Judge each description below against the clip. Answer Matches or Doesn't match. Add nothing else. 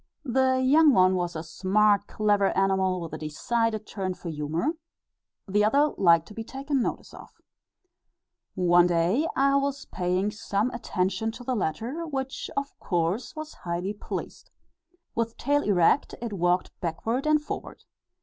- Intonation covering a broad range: Matches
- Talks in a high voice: Matches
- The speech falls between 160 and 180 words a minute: Doesn't match